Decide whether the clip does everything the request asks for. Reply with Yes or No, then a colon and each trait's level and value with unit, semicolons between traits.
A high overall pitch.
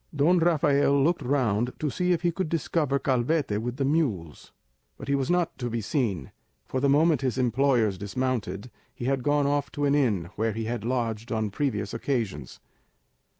No: low, 130 Hz